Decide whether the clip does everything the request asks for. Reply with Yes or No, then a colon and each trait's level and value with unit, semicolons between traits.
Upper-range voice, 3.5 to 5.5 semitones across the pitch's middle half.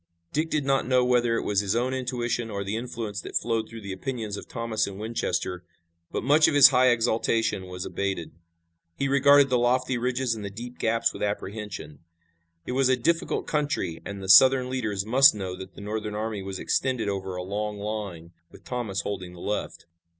No: low, 115 Hz; average, 4.2 semitones